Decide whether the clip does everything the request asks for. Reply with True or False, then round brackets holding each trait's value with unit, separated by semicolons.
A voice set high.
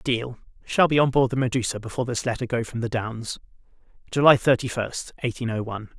False (120 Hz)